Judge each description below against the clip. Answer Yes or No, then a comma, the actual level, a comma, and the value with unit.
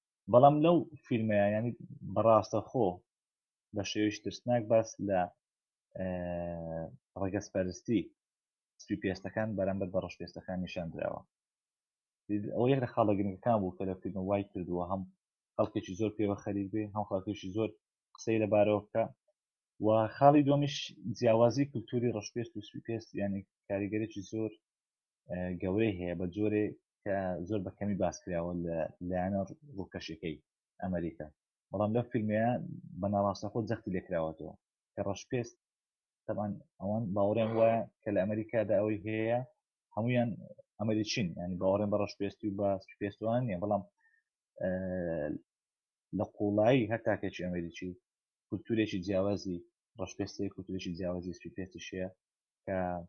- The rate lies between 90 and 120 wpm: Yes, average, 115 wpm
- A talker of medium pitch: No, low, 100 Hz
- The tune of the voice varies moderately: Yes, average, 3.2 semitones